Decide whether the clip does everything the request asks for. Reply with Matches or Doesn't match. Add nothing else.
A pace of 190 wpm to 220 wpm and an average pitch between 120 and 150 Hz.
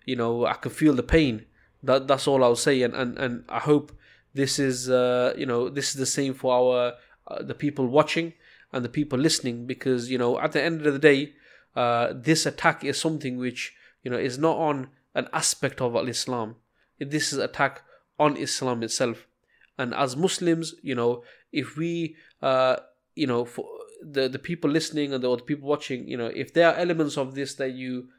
Matches